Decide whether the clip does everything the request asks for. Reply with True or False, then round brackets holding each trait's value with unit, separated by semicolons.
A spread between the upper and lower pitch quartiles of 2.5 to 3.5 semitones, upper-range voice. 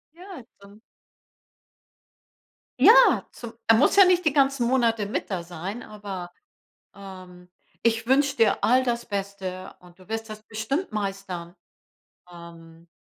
False (4.7 semitones; 210 Hz)